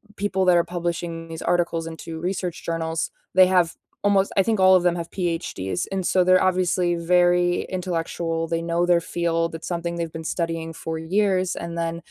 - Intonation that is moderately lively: No, narrow, 1.7 semitones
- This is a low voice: No, medium, 170 Hz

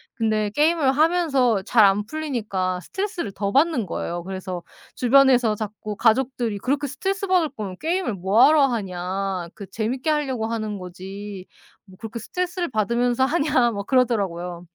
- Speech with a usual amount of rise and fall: No, wide, 6.1 semitones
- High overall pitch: Yes, high, 230 Hz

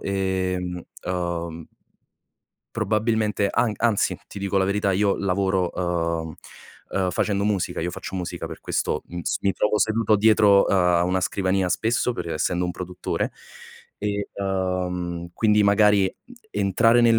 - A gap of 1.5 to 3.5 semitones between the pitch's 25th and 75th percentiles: Yes, narrow, 2.6 semitones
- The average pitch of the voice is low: Yes, very low, 95 Hz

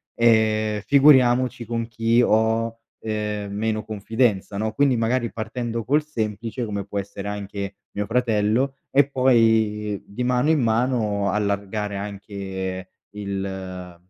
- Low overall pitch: Yes, low, 110 Hz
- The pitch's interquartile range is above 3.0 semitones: No, average, 2.7 semitones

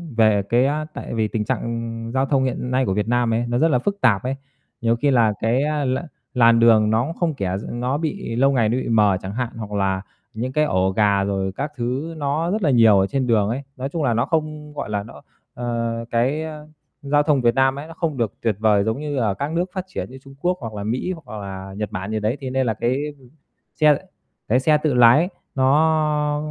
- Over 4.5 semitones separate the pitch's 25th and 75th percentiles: Yes, average, 4.9 semitones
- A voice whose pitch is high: No, low, 125 Hz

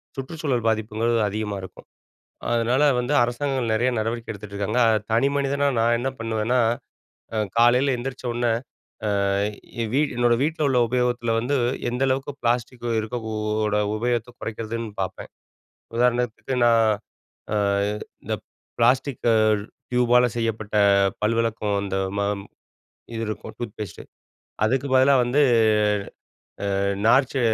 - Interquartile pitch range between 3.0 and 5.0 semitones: No, narrow, 2.4 semitones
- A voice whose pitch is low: Yes, low, 120 Hz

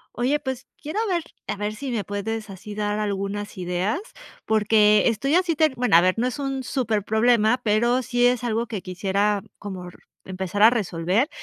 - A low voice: No, high, 215 Hz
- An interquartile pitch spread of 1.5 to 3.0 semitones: No, average, 3.5 semitones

